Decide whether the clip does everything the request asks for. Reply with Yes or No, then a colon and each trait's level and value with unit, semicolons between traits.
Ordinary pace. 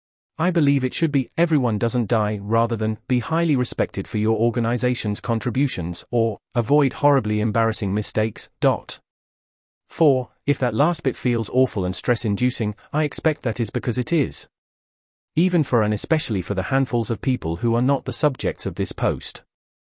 Yes: average, 170 wpm